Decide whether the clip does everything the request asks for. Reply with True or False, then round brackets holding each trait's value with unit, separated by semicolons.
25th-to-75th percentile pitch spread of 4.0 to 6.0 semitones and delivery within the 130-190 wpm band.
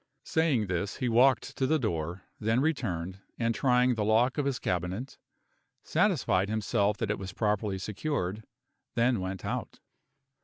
True (4.7 semitones; 150 wpm)